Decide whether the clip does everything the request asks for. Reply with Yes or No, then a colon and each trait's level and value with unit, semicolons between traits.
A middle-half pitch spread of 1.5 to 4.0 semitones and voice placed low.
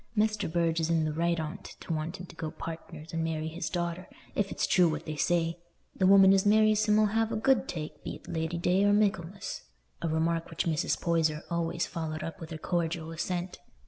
No: average, 2.9 semitones; medium, 170 Hz